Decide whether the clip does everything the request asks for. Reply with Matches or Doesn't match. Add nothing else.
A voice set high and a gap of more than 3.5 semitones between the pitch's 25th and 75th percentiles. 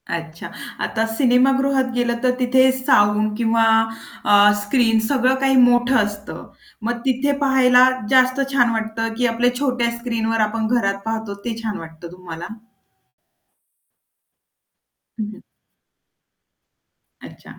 Doesn't match